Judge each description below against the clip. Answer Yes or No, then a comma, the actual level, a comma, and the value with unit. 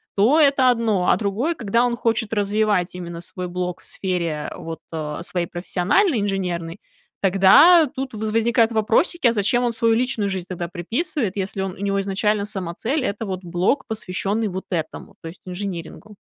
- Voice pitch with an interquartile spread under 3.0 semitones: No, average, 4.2 semitones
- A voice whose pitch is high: Yes, high, 200 Hz